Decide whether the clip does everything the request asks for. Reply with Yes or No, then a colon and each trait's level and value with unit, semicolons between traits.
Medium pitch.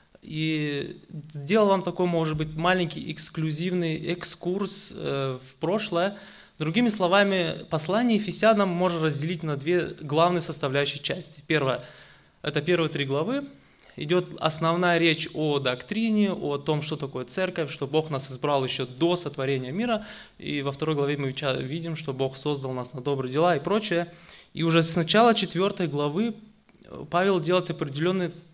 Yes: medium, 165 Hz